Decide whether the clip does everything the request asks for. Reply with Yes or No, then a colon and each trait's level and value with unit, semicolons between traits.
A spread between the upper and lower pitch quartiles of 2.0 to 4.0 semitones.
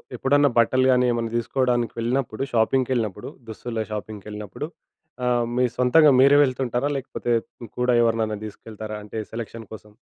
Yes: average, 2.7 semitones